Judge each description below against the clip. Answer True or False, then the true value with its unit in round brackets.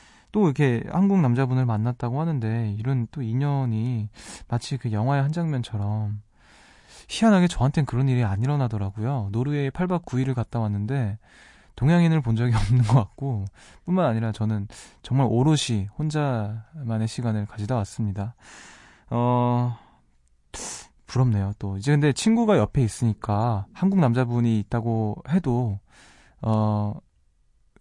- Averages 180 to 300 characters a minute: True (290 characters per minute)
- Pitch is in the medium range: False (120 Hz)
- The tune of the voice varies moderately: True (4.3 semitones)